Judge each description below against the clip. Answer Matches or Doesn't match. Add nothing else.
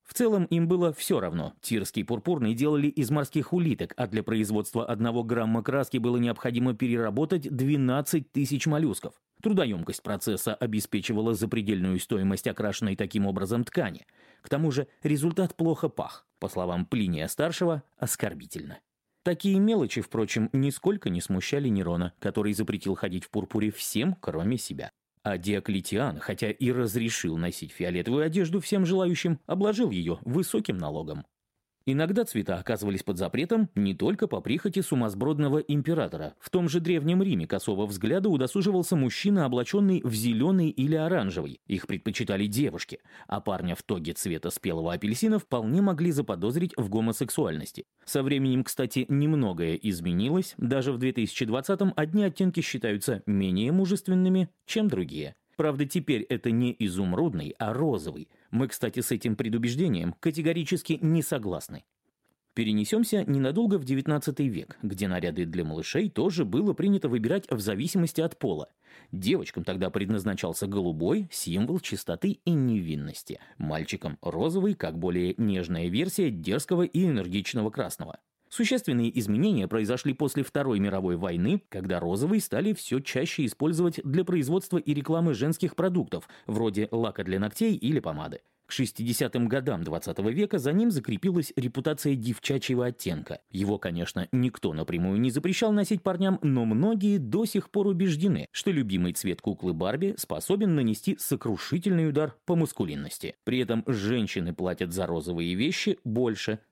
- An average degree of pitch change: Doesn't match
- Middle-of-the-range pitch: Doesn't match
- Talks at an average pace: Matches